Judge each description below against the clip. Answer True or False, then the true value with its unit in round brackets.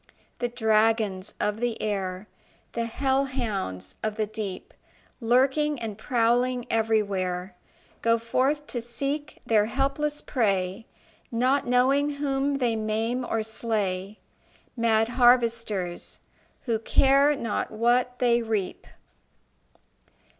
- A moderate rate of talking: False (110 wpm)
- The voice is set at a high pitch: True (230 Hz)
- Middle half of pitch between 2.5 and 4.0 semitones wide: True (3.0 semitones)